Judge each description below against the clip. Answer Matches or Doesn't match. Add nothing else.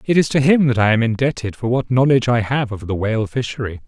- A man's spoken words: Matches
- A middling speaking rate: Doesn't match